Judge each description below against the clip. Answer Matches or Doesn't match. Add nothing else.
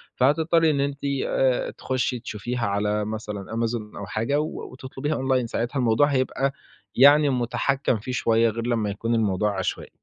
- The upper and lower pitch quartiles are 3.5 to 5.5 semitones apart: Matches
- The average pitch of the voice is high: Doesn't match